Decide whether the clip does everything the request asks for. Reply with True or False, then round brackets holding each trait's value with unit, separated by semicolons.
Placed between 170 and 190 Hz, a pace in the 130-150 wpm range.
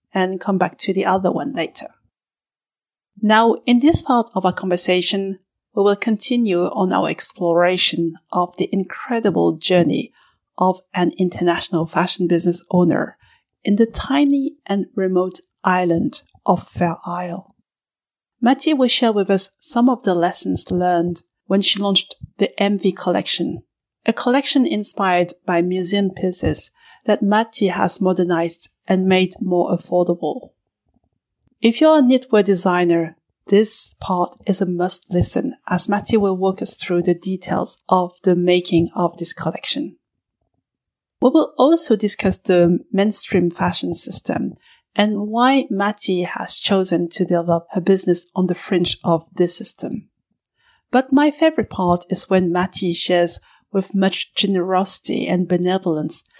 True (185 Hz; 140 wpm)